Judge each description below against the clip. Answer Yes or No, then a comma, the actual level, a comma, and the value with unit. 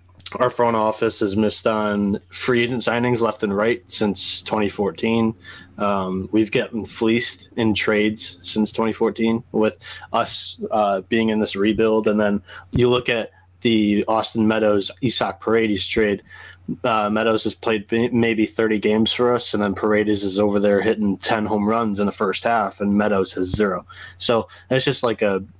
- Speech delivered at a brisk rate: No, average, 170 wpm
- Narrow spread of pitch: Yes, narrow, 1.9 semitones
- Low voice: Yes, low, 110 Hz